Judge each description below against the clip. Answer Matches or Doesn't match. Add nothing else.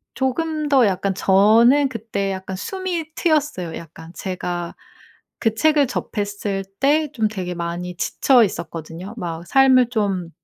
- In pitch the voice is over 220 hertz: Doesn't match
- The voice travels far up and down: Matches